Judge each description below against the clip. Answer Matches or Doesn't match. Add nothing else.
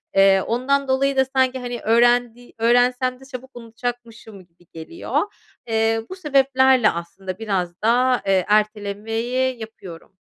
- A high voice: Matches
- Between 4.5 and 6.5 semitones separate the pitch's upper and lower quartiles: Doesn't match